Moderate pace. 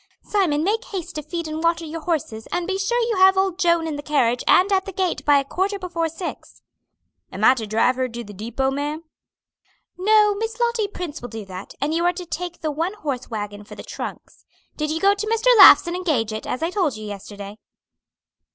No: fast, 225 wpm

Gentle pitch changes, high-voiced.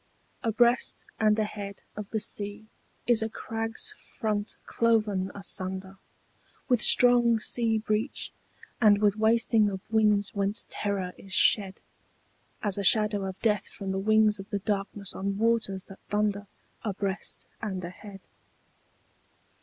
Yes: narrow, 1.9 semitones; high, 210 Hz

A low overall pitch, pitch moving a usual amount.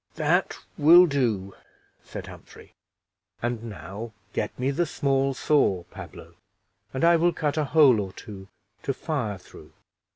No: low, 130 Hz; wide, 6.4 semitones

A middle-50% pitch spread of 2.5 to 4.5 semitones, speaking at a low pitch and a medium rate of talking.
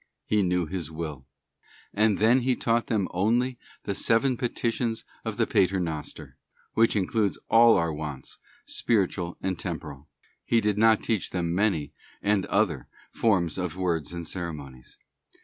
No: average, 5.1 semitones; very low, 95 Hz; average, 150 wpm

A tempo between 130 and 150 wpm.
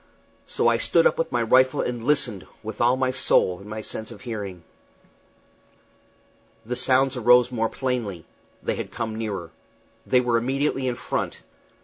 No: average, 160 wpm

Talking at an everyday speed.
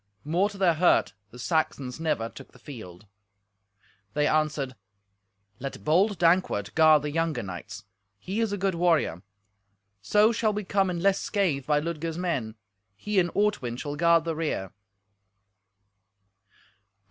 Yes: average, 145 wpm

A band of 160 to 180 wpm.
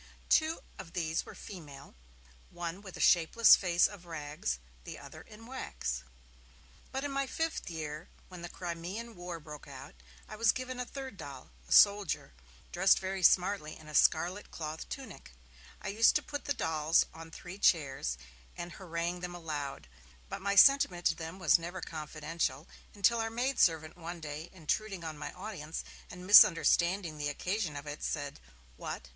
Yes: average, 170 wpm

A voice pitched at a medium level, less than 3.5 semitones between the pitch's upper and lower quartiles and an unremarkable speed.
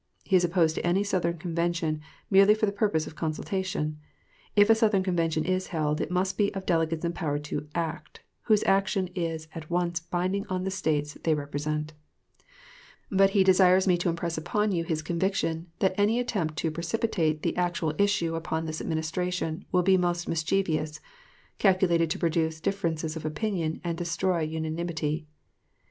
Yes: medium, 170 Hz; average, 2.9 semitones; average, 165 wpm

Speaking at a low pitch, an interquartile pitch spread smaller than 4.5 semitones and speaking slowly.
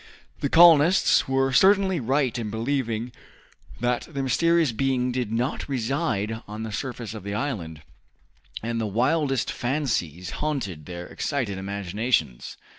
No: low, 120 Hz; average, 4.8 semitones; slow, 130 wpm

